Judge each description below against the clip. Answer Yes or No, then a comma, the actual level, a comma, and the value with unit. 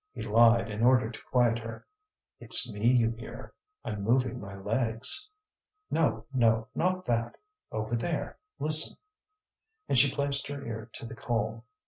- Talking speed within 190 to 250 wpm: No, average, 150 wpm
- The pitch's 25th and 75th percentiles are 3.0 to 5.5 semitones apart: No, narrow, 2.4 semitones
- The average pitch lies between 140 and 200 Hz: No, low, 115 Hz